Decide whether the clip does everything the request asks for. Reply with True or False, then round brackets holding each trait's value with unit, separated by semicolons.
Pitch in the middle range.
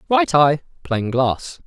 True (150 Hz)